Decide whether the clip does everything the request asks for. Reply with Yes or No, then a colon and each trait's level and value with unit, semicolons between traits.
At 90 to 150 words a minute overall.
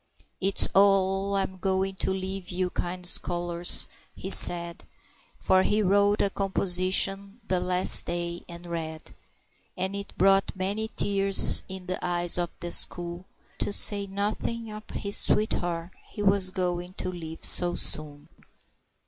Yes: average, 145 wpm